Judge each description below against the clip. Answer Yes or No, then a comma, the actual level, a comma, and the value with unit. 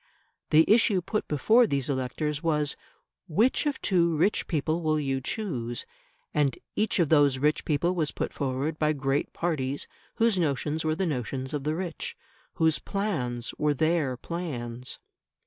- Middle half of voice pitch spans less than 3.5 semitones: No, average, 4.0 semitones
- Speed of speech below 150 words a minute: No, average, 155 wpm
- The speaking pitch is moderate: Yes, medium, 150 Hz